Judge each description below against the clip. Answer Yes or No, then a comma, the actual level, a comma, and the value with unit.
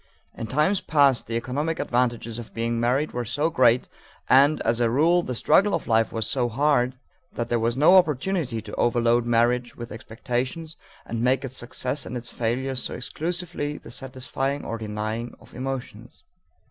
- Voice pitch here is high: No, low, 125 Hz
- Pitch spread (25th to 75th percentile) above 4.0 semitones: No, average, 3.3 semitones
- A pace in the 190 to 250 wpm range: No, average, 170 wpm